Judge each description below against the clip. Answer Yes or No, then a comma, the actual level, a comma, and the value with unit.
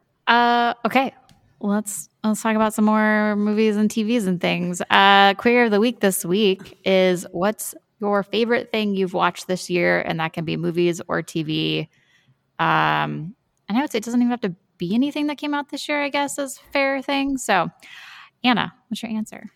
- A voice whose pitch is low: No, high, 215 Hz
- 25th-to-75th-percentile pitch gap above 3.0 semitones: Yes, average, 4.6 semitones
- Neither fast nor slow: Yes, average, 195 wpm